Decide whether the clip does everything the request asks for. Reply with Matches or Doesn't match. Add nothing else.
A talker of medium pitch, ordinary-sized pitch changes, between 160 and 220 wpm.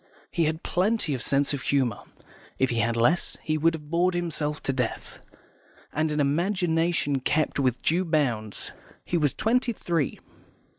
Matches